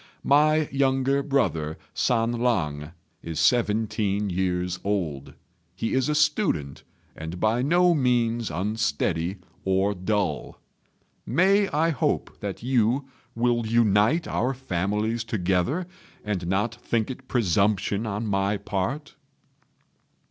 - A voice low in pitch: Yes, low, 110 Hz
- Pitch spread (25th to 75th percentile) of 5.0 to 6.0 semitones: Yes, wide, 5.5 semitones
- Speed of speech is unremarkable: No, slow, 110 wpm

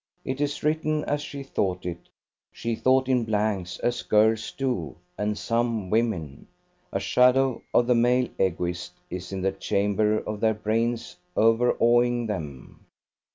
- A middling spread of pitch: Yes, average, 4.1 semitones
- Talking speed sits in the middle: Yes, average, 145 wpm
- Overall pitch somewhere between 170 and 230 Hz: No, low, 115 Hz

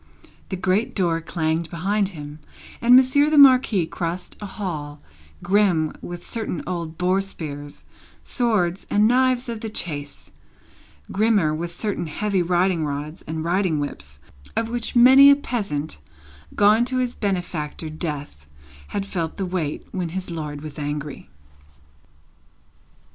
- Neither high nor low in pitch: Yes, medium, 180 Hz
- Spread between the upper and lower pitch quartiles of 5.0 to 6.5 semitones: Yes, average, 5.3 semitones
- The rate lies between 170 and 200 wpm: No, slow, 135 wpm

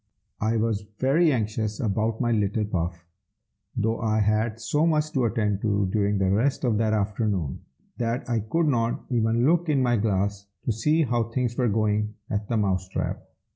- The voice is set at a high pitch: No, low, 110 Hz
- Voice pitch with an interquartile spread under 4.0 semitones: Yes, average, 2.7 semitones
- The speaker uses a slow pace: No, average, 180 wpm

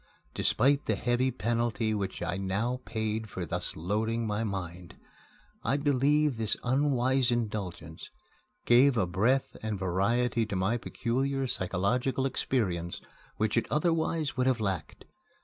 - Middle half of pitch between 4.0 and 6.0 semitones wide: Yes, average, 4.8 semitones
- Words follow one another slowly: Yes, slow, 130 wpm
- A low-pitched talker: Yes, low, 115 Hz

